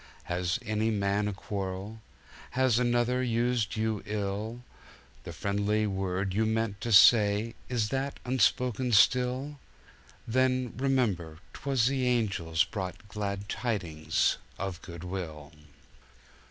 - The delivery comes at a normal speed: No, slow, 115 wpm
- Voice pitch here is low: Yes, low, 105 Hz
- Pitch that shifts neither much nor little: Yes, average, 4.0 semitones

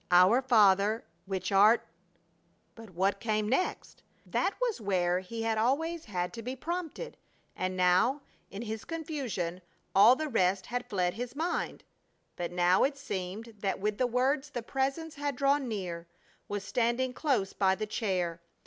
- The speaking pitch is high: Yes, high, 220 Hz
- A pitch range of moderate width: No, wide, 5.9 semitones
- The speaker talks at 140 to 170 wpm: Yes, average, 160 wpm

